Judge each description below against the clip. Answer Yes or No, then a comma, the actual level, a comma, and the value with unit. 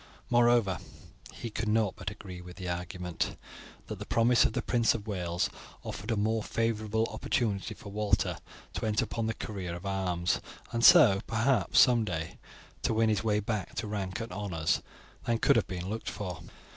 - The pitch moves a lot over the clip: No, average, 3.4 semitones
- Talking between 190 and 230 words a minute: No, average, 180 wpm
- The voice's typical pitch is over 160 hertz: No, low, 105 Hz